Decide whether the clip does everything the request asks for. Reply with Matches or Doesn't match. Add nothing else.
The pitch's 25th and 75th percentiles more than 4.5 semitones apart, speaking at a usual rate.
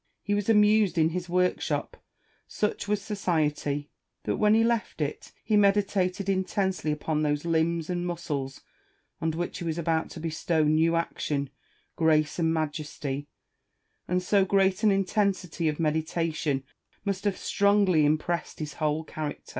Doesn't match